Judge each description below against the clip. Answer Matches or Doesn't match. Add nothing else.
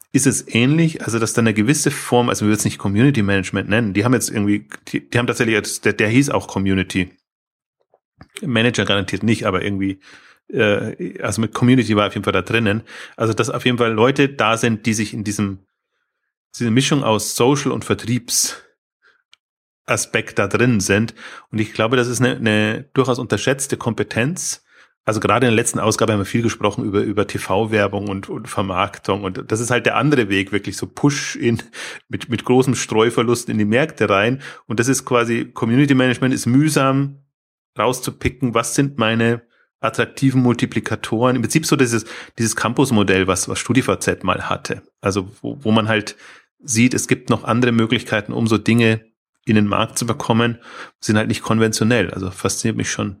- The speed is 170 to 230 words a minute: Matches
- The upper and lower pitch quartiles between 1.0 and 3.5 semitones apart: Matches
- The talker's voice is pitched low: Matches